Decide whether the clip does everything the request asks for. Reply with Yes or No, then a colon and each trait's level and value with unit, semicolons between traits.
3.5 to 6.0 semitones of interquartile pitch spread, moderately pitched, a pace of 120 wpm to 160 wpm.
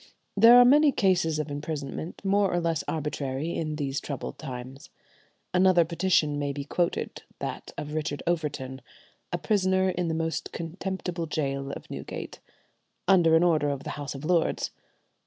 Yes: average, 3.9 semitones; medium, 160 Hz; average, 155 wpm